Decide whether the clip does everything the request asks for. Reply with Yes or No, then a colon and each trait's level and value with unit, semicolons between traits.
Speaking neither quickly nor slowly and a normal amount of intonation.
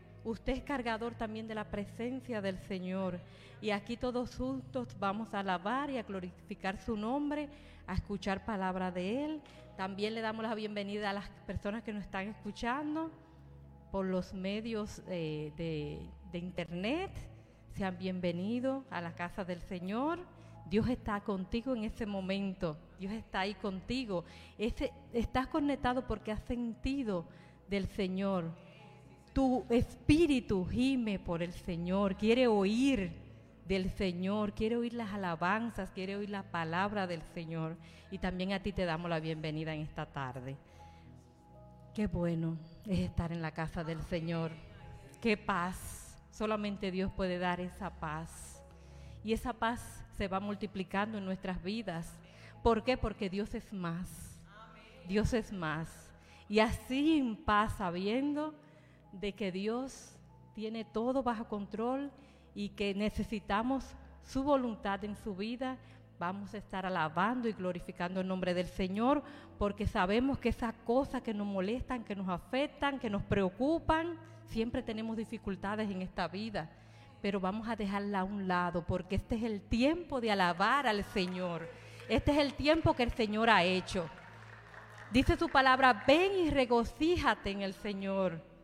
Yes: average, 150 wpm; average, 4.5 semitones